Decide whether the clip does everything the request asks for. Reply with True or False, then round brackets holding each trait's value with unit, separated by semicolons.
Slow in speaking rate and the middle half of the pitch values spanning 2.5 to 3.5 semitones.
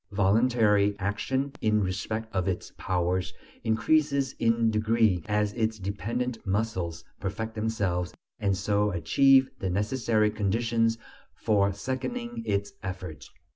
True (115 wpm; 2.8 semitones)